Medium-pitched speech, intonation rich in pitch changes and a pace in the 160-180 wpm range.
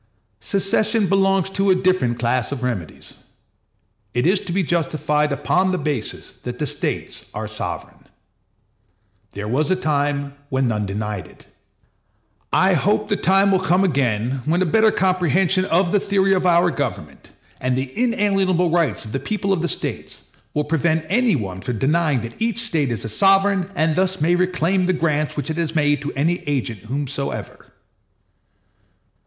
Yes: medium, 165 Hz; wide, 5.8 semitones; average, 170 wpm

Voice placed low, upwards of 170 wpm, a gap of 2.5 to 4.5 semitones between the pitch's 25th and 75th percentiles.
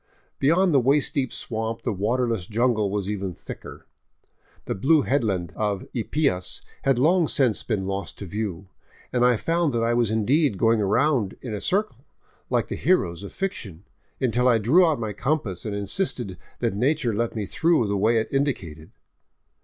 No: low, 115 Hz; average, 180 wpm; average, 5.3 semitones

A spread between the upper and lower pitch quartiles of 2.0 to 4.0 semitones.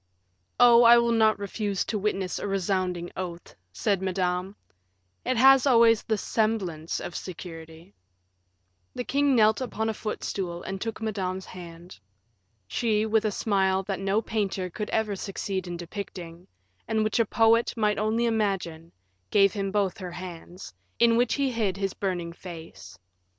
Yes: average, 3.4 semitones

